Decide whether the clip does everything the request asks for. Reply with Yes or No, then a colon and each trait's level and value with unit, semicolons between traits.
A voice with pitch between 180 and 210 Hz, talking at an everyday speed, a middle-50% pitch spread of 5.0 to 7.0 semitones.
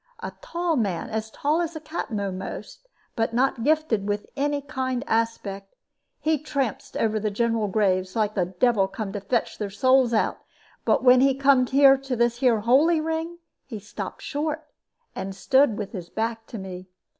No: high, 235 Hz; average, 175 wpm; average, 5.3 semitones